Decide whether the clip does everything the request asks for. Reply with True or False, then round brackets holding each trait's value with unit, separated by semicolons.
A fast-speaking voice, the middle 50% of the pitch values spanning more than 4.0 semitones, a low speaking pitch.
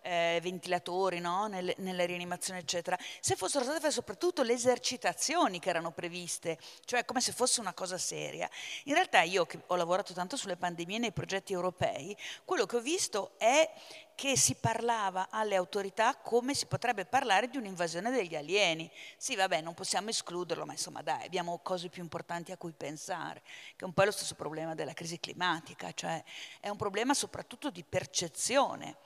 False (180 wpm; 5.5 semitones; 185 Hz)